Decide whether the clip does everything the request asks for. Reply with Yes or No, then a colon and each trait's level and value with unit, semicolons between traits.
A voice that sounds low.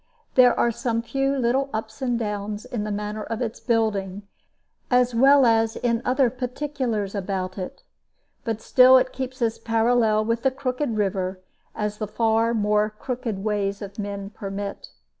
No: high, 225 Hz